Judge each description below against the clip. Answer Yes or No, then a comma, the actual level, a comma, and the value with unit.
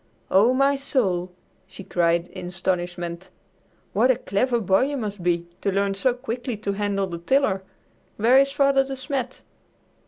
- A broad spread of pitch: Yes, wide, 5.9 semitones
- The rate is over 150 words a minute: Yes, average, 160 wpm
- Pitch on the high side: Yes, high, 205 Hz